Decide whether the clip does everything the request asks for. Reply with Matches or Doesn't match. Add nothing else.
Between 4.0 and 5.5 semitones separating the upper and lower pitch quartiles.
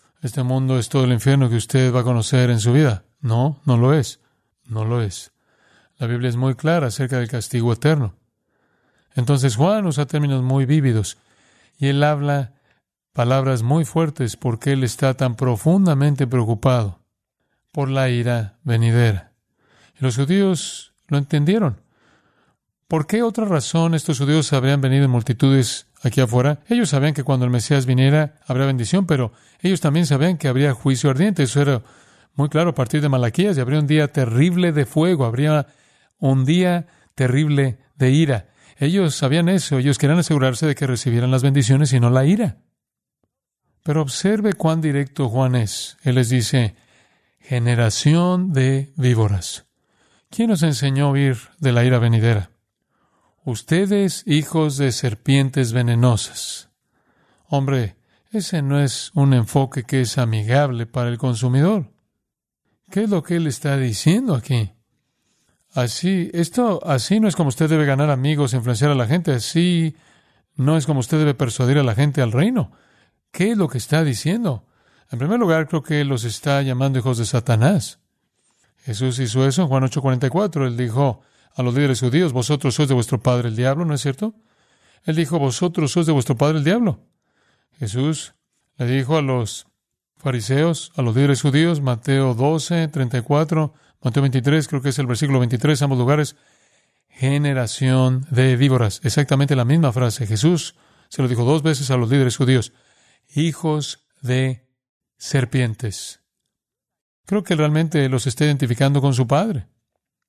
Doesn't match